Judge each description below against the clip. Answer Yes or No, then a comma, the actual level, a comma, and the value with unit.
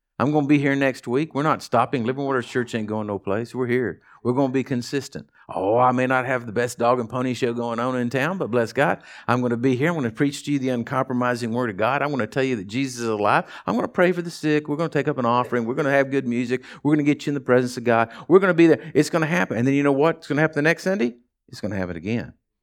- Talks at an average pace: No, fast, 325 wpm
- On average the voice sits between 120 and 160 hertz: Yes, low, 130 Hz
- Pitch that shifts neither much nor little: Yes, average, 3.2 semitones